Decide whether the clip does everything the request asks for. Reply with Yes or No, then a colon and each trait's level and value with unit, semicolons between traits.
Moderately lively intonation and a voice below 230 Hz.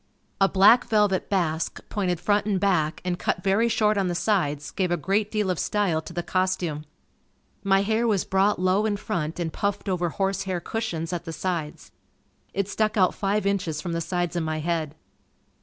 Yes: average, 3.1 semitones; medium, 185 Hz